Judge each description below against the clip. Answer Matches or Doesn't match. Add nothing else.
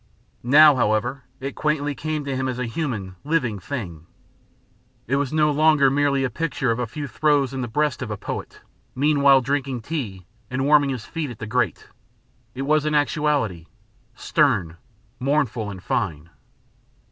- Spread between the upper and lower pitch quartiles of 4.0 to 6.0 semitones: Matches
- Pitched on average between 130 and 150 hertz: Matches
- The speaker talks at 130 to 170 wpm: Matches